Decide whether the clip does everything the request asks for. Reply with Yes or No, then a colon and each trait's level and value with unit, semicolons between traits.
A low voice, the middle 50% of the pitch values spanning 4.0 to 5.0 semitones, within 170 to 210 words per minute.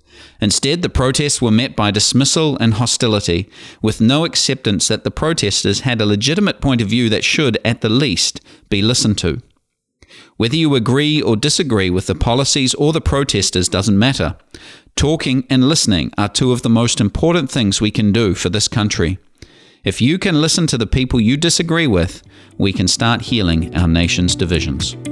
No: low, 115 Hz; wide, 5.4 semitones; average, 180 wpm